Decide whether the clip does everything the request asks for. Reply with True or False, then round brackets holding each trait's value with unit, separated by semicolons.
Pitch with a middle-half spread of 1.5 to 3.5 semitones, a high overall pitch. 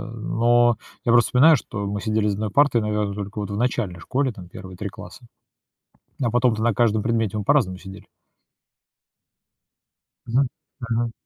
False (2.8 semitones; 110 Hz)